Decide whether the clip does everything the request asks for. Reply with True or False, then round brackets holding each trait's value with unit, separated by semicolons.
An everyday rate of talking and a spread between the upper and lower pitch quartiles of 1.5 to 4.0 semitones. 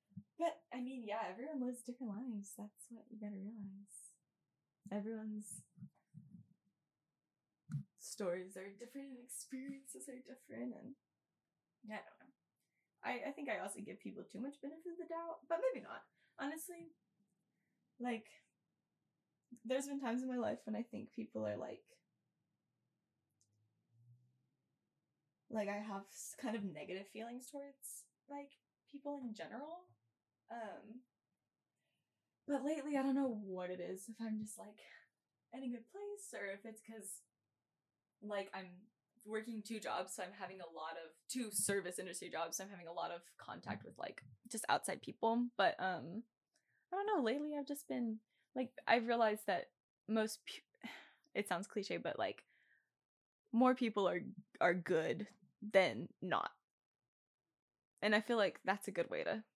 False (155 wpm; 4.9 semitones)